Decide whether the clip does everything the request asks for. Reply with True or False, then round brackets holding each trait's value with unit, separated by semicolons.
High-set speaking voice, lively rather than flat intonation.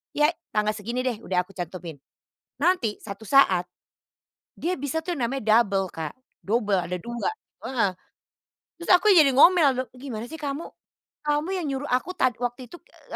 True (250 Hz; 5.9 semitones)